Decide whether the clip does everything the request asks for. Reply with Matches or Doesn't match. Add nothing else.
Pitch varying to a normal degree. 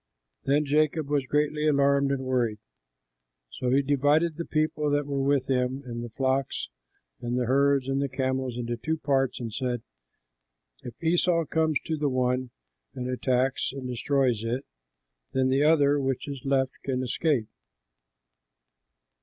Doesn't match